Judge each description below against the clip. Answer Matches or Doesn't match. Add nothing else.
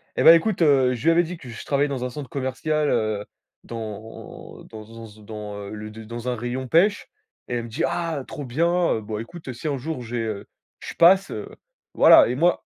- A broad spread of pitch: Matches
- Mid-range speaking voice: Doesn't match